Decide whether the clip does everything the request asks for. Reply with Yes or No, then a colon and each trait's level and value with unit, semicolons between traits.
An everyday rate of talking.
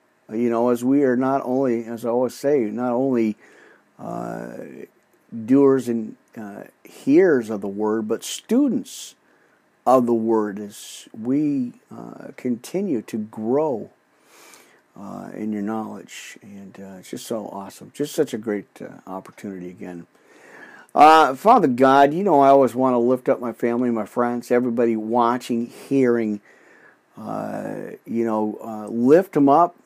Yes: average, 150 wpm